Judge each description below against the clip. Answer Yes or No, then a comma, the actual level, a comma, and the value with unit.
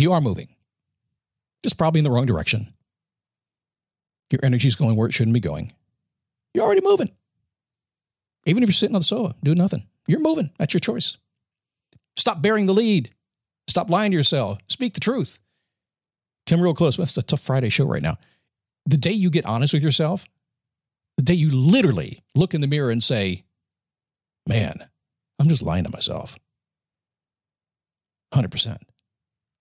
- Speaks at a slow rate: No, average, 165 wpm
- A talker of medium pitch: Yes, medium, 155 Hz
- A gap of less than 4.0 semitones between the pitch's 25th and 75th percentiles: No, average, 5.2 semitones